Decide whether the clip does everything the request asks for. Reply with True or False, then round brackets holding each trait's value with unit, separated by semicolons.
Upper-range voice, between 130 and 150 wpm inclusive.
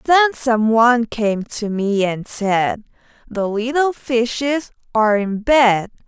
True (230 Hz; 140 wpm)